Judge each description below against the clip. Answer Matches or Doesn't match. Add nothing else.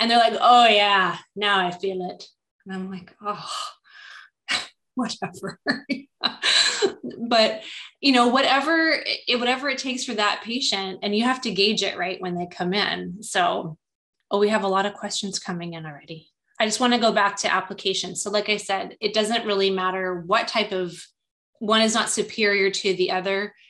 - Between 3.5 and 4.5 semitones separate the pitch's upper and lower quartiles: Matches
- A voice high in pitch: Matches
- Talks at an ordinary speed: Matches